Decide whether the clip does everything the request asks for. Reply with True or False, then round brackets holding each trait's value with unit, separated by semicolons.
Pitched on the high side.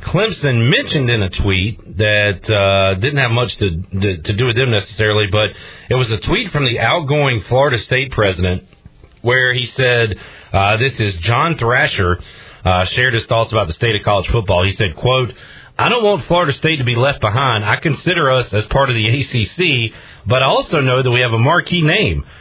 False (120 Hz)